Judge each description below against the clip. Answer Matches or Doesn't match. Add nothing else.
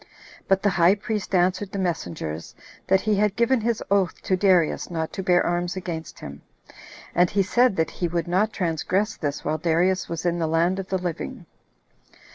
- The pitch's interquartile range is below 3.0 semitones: Matches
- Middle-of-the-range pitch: Matches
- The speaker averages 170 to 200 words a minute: Matches